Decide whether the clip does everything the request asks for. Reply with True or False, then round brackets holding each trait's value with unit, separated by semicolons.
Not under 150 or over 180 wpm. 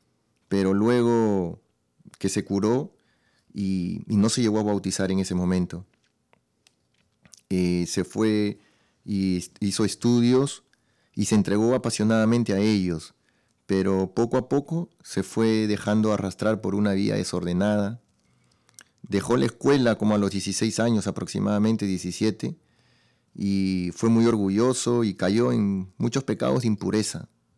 False (130 wpm)